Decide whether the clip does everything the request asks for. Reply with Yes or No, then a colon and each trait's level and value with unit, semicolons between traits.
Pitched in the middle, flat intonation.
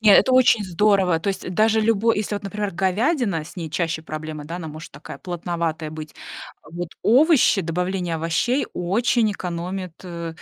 No: medium, 180 Hz; average, 4.2 semitones